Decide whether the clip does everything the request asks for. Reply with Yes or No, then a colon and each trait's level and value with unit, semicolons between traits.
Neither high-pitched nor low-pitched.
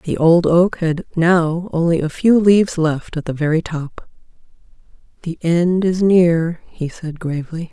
Yes: medium, 170 Hz